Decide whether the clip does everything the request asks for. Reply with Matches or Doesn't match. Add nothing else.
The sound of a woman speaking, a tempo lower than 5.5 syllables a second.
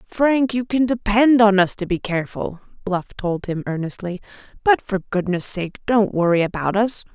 Matches